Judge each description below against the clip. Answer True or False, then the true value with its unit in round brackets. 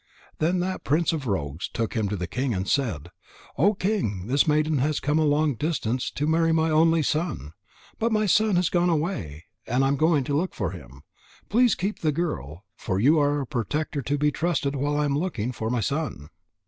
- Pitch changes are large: True (6.3 semitones)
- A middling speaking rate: False (210 wpm)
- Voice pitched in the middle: True (145 Hz)